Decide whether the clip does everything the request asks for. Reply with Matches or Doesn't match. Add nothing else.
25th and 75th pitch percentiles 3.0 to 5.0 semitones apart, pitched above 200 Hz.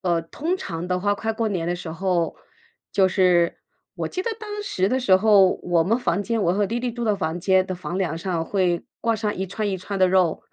Doesn't match